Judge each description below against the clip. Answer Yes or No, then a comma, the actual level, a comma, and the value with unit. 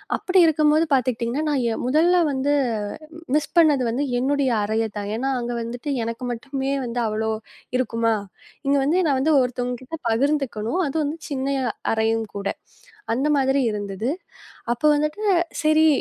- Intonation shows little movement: No, average, 4.1 semitones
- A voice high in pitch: Yes, very high, 260 Hz